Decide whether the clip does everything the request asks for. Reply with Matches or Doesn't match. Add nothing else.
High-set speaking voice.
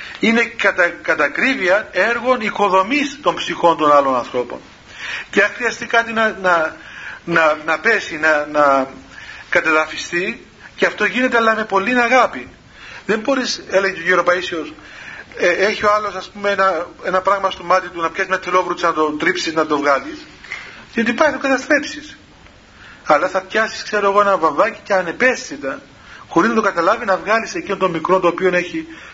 Matches